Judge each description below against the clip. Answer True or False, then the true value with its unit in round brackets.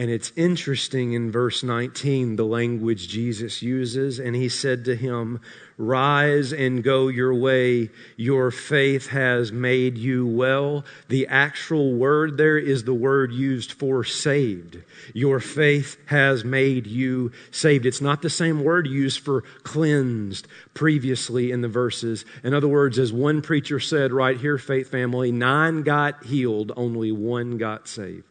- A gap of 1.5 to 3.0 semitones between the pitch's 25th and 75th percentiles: True (2.7 semitones)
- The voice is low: True (130 Hz)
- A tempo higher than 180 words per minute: False (155 wpm)